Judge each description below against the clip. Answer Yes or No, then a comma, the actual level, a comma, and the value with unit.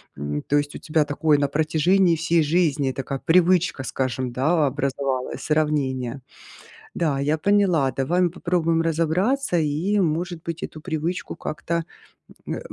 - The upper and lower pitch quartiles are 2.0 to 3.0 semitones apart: No, average, 3.5 semitones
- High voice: No, medium, 155 Hz